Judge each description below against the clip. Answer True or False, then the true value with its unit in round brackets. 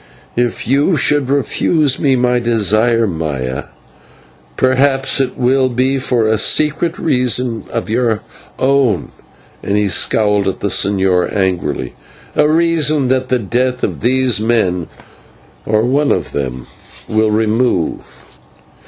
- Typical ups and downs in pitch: True (4.2 semitones)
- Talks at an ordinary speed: False (130 wpm)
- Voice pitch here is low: True (120 Hz)